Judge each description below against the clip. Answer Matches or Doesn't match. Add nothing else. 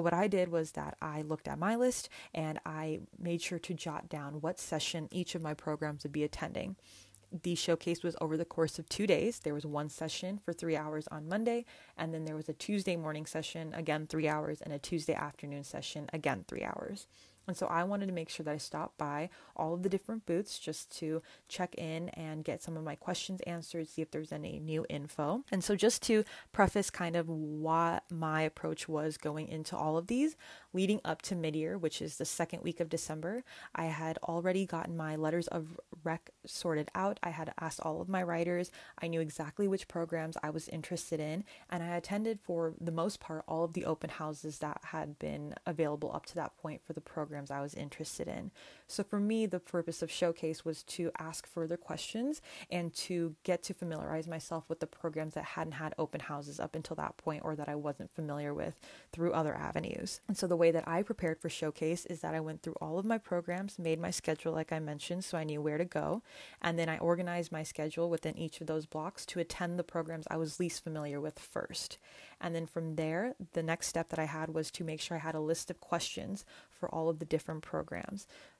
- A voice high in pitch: Doesn't match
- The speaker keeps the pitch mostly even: Matches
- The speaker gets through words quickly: Matches